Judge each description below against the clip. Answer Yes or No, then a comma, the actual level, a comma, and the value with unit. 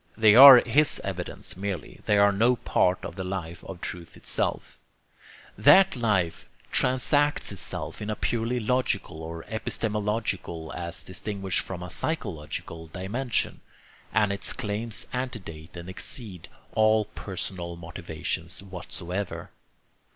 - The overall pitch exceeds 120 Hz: No, low, 100 Hz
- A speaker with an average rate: No, slow, 120 wpm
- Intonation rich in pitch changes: No, average, 4.3 semitones